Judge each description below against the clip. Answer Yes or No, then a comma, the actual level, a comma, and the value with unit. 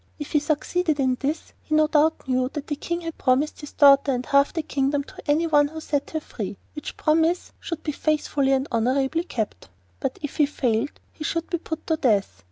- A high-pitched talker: Yes, very high, 295 Hz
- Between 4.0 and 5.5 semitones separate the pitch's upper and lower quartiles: No, average, 2.8 semitones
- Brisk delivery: Yes, fast, 210 wpm